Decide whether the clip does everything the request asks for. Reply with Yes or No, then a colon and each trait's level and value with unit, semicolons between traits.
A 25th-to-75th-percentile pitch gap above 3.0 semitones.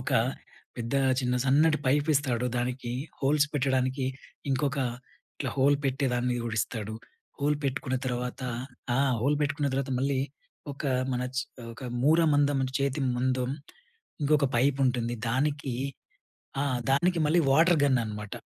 No: narrow, 2.4 semitones